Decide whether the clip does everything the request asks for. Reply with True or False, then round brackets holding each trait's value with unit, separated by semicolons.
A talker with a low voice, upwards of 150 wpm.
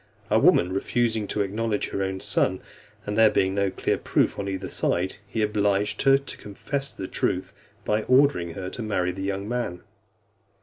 True (100 Hz; 180 wpm)